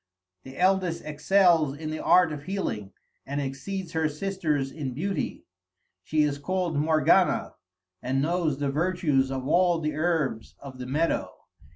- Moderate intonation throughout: Yes, average, 4.1 semitones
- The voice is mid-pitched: Yes, medium, 155 Hz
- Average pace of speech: Yes, average, 150 wpm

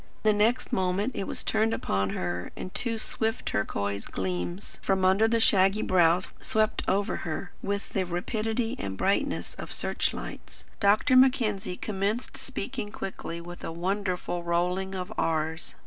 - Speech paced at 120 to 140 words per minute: No, average, 150 wpm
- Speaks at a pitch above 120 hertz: Yes, high, 190 Hz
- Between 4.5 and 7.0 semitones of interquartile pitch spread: No, average, 3.9 semitones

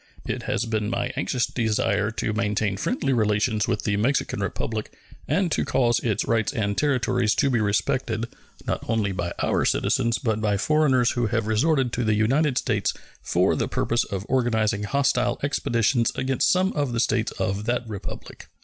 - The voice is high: No, low, 115 Hz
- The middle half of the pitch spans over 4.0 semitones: No, average, 3.2 semitones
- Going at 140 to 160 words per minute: No, average, 175 wpm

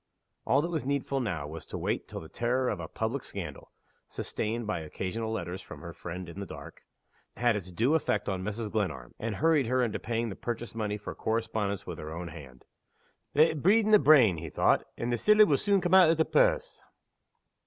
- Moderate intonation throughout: No, wide, 7.2 semitones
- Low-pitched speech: Yes, low, 115 Hz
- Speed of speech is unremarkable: No, fast, 220 wpm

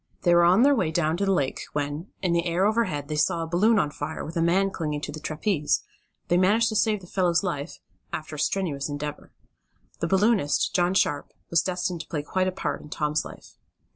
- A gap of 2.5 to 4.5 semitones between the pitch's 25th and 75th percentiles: Yes, average, 4.0 semitones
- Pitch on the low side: No, medium, 170 Hz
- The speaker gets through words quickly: Yes, fast, 220 wpm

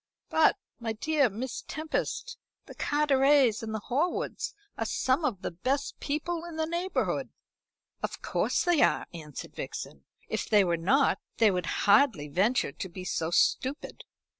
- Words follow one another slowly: No, average, 155 wpm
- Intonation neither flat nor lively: No, wide, 7.9 semitones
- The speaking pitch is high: Yes, very high, 260 Hz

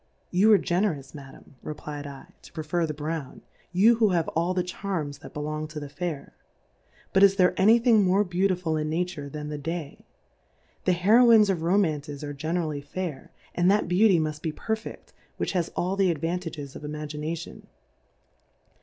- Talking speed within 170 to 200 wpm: Yes, average, 180 wpm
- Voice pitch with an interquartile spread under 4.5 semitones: Yes, average, 3.8 semitones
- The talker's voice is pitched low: No, medium, 165 Hz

